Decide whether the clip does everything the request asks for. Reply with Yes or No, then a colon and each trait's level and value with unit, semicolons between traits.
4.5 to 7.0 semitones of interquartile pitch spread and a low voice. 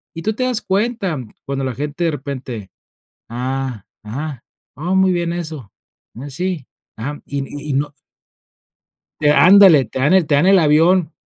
No: average, 4.9 semitones; medium, 150 Hz